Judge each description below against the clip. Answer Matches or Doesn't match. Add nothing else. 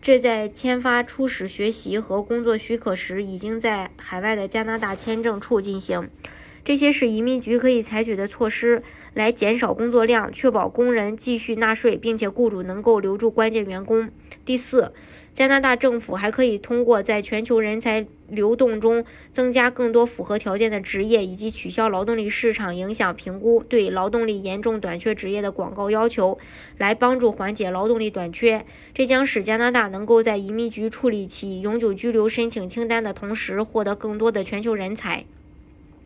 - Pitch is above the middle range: Matches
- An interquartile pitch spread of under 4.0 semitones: Matches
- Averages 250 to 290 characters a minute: Matches